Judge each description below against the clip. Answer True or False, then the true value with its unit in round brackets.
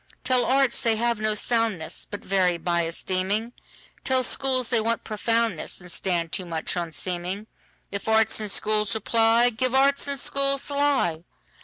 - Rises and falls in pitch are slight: False (5.0 semitones)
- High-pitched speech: True (220 Hz)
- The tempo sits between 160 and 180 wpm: False (140 wpm)